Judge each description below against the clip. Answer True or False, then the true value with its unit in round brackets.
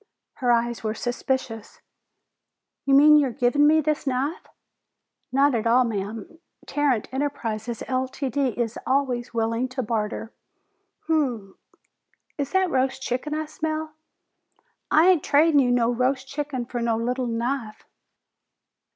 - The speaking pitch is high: True (255 Hz)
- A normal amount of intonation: True (3.6 semitones)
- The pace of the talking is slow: True (130 wpm)